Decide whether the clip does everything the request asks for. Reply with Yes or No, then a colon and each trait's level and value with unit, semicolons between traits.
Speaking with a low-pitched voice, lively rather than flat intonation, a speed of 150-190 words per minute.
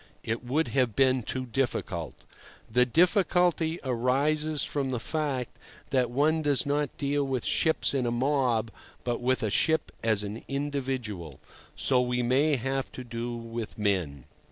No: low, 130 Hz; average, 3.5 semitones; average, 155 wpm